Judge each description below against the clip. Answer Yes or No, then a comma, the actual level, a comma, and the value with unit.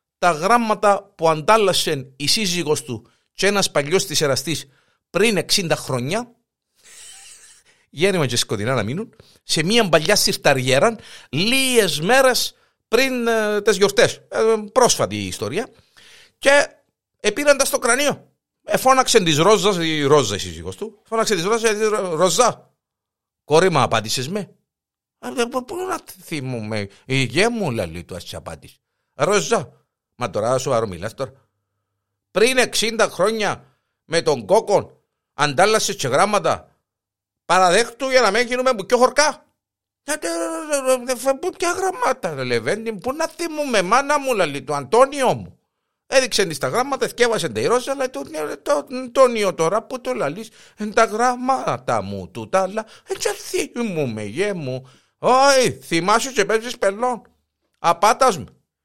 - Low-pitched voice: No, high, 210 Hz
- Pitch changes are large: Yes, wide, 9.0 semitones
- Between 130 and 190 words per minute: Yes, average, 135 wpm